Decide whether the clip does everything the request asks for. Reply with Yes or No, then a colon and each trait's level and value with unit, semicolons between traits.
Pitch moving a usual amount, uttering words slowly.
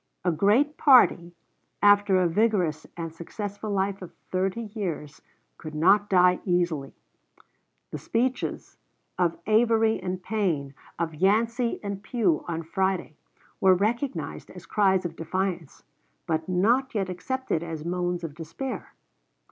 Yes: average, 4.0 semitones; slow, 130 wpm